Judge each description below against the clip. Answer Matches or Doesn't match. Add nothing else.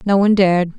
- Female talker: Matches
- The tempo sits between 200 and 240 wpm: Matches